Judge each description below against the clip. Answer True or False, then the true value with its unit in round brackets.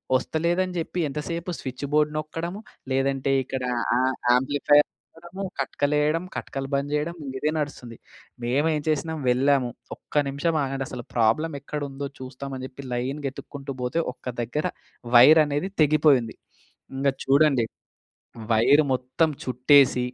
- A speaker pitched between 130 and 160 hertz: True (140 Hz)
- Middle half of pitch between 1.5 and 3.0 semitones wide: True (2.7 semitones)